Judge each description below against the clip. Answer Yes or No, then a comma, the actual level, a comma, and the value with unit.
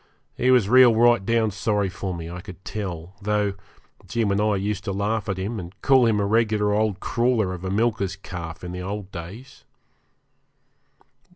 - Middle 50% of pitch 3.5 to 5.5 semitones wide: No, average, 3.0 semitones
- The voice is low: Yes, low, 100 Hz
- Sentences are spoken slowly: No, average, 180 wpm